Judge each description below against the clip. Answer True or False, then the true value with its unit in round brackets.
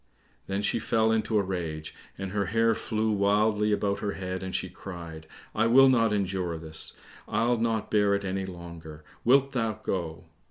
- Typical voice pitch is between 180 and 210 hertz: False (100 Hz)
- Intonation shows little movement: False (3.4 semitones)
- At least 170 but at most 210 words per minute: True (175 wpm)